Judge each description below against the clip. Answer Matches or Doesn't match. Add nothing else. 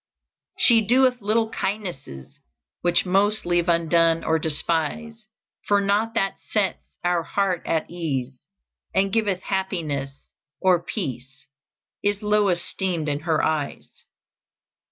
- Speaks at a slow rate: Matches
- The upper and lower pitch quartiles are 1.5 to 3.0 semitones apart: Doesn't match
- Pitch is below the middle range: Doesn't match